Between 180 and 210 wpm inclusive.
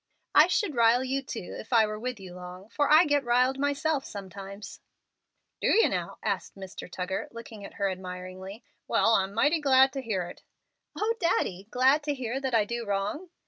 Yes: average, 190 wpm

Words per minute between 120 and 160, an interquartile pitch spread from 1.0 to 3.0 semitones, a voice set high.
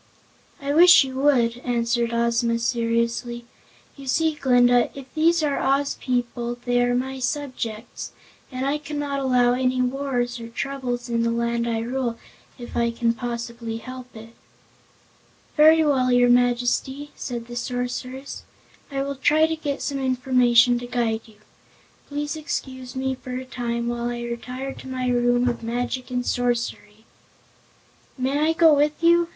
Yes: average, 155 wpm; narrow, 2.4 semitones; very high, 250 Hz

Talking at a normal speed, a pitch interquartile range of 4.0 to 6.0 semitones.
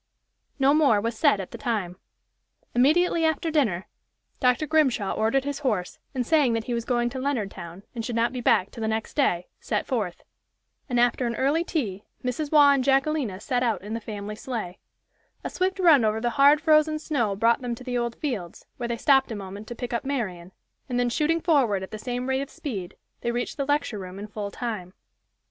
No: fast, 210 wpm; average, 4.7 semitones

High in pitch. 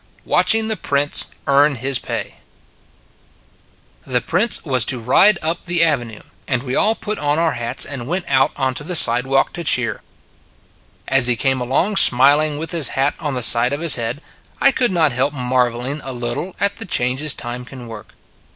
No: low, 135 Hz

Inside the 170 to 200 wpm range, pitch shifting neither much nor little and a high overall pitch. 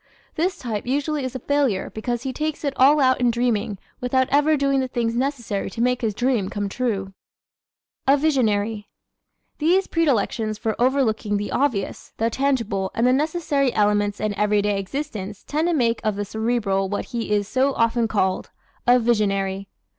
Yes: average, 175 wpm; average, 4.8 semitones; high, 235 Hz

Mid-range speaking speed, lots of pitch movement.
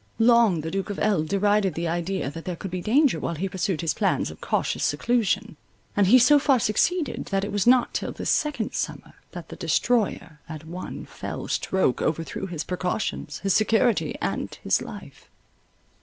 No: average, 180 wpm; average, 5.0 semitones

